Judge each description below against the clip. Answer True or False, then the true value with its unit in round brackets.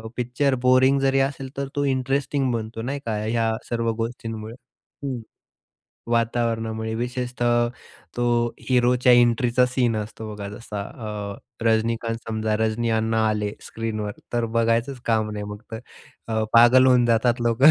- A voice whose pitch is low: True (115 Hz)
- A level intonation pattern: True (1.9 semitones)